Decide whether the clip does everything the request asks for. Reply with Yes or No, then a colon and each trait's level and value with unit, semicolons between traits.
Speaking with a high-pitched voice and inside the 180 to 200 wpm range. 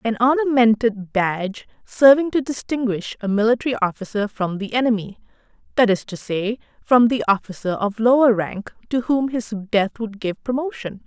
No: high, 225 Hz; average, 150 wpm